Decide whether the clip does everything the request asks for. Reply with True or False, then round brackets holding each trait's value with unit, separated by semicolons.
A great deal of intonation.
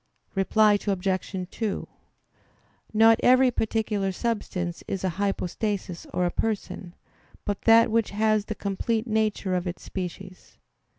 False (2.9 semitones)